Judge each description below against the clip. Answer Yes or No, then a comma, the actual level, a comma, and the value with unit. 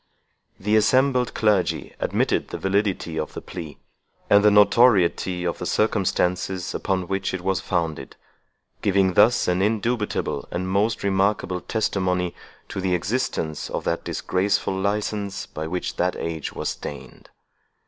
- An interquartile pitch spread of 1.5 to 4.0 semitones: Yes, narrow, 2.6 semitones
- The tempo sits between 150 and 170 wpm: No, average, 140 wpm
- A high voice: No, very low, 95 Hz